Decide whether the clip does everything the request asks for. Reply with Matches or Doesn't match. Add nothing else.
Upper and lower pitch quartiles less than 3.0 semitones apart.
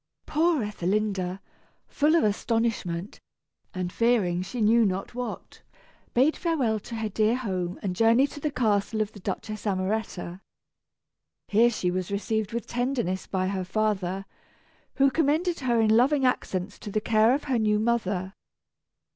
Doesn't match